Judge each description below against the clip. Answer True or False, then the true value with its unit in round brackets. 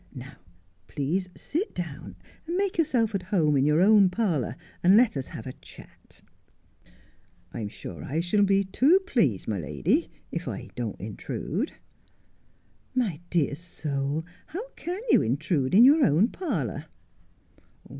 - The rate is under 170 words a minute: True (150 wpm)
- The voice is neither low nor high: True (180 Hz)